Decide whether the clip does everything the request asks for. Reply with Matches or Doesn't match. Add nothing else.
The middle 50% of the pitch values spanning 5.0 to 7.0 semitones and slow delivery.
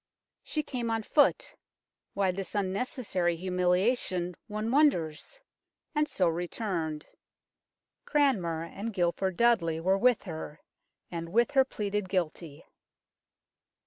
Matches